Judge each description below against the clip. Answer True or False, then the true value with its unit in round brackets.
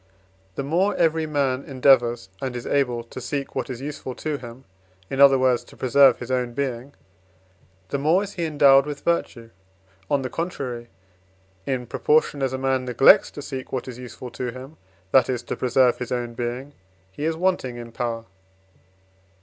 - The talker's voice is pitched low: True (130 Hz)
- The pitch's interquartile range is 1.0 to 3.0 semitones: True (2.6 semitones)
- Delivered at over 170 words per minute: True (180 wpm)